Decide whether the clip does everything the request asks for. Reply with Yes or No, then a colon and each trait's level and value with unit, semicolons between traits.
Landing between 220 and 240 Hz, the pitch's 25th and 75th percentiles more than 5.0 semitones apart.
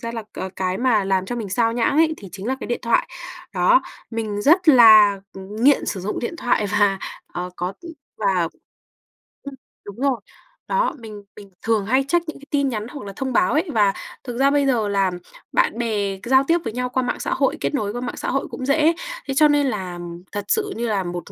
Yes: high, 230 Hz; wide, 5.4 semitones